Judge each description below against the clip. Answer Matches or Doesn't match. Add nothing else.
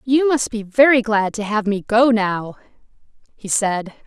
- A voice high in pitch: Matches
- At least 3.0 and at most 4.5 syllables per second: Matches